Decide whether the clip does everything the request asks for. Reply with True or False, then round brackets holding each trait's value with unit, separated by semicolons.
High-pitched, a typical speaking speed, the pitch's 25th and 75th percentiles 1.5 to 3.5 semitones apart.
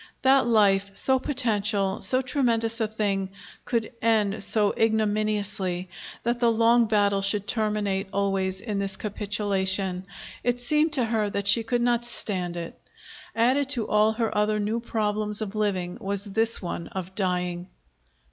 True (210 Hz; 150 wpm; 2.7 semitones)